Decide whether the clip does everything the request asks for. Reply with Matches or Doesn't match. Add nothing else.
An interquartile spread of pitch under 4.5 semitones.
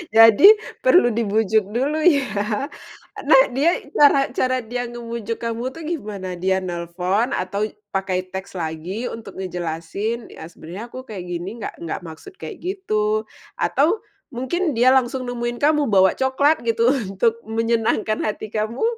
Doesn't match